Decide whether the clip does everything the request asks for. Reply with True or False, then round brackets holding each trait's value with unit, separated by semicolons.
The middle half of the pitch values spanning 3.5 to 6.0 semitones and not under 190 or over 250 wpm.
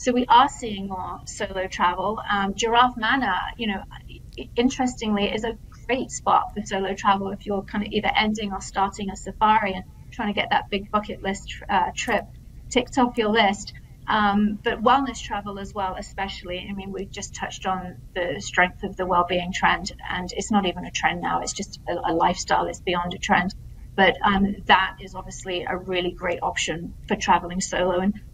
False (2.4 semitones; 195 wpm)